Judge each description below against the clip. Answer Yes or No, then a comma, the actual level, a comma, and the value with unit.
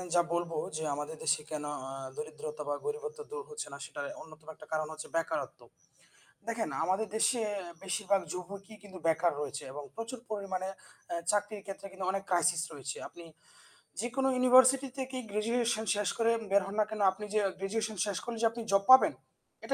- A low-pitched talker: No, high, 195 Hz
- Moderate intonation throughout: No, wide, 5.8 semitones